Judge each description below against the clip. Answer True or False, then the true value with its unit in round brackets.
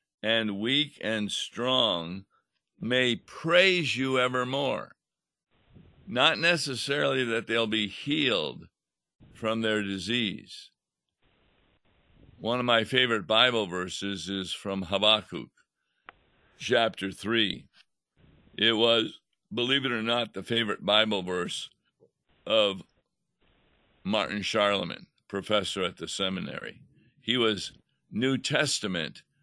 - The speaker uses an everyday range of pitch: True (3.9 semitones)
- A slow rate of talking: True (100 wpm)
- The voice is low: True (115 Hz)